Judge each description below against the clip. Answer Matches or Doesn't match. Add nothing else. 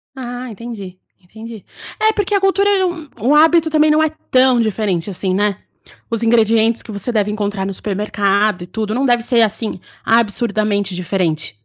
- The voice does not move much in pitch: Doesn't match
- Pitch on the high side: Matches